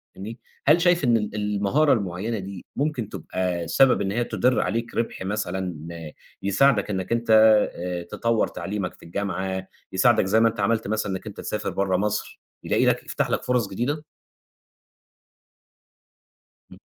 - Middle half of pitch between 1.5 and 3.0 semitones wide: No, average, 3.5 semitones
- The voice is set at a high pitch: No, low, 105 Hz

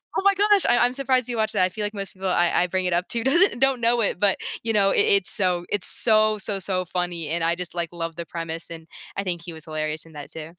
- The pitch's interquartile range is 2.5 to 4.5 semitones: No, average, 4.9 semitones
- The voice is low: No, medium, 185 Hz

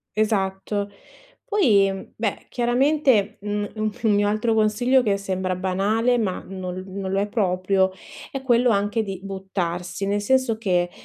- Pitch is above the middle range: Yes, high, 205 Hz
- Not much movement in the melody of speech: No, average, 3.0 semitones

